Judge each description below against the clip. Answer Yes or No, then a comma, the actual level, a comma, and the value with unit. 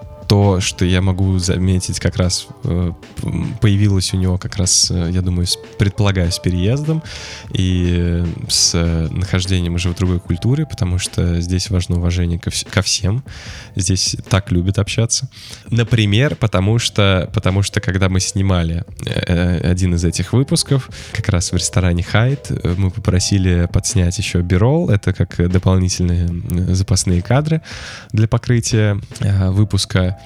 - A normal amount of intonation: Yes, average, 3.5 semitones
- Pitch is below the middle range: Yes, very low, 95 Hz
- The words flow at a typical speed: Yes, average, 135 wpm